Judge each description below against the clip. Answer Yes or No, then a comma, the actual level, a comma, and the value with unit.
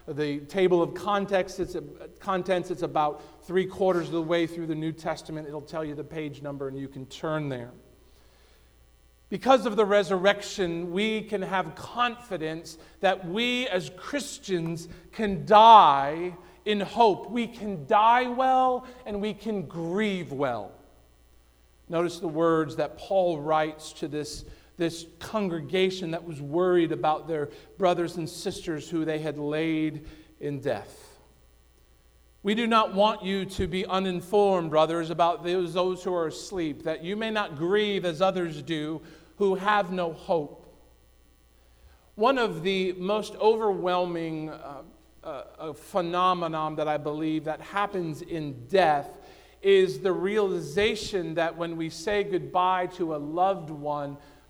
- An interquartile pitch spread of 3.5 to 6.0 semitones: Yes, average, 3.9 semitones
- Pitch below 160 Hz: No, medium, 170 Hz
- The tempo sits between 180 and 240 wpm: No, average, 145 wpm